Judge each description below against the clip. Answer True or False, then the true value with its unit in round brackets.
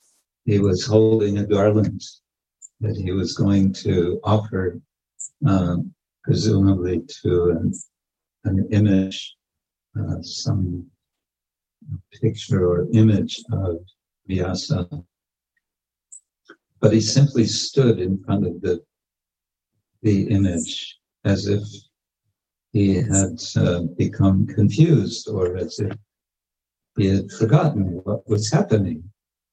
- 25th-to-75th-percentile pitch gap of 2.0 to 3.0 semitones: False (3.6 semitones)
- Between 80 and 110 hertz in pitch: True (95 Hz)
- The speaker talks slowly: True (100 wpm)